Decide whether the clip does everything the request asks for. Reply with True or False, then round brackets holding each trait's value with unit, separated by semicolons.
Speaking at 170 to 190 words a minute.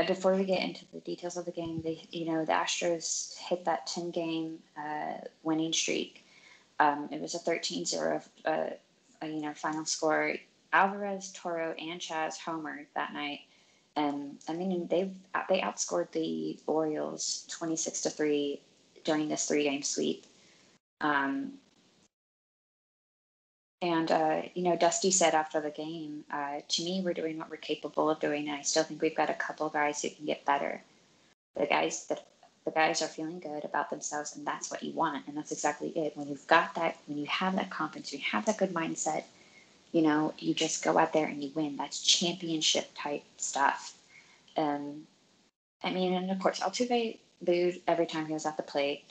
True (185 wpm)